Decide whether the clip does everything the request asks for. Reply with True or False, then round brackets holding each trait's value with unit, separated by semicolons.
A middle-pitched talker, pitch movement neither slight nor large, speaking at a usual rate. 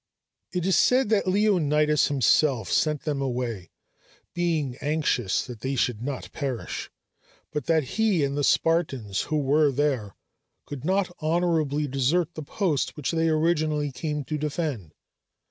True (150 Hz; 3.5 semitones; 145 wpm)